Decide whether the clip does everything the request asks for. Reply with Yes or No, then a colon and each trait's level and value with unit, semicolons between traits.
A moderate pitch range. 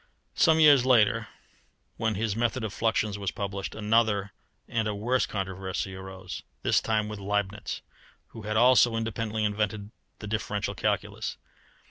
No: narrow, 2.0 semitones